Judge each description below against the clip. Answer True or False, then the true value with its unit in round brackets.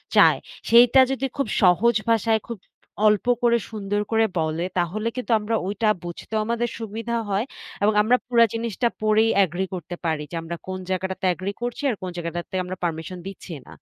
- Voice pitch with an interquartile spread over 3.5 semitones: True (4.2 semitones)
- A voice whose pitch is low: False (210 Hz)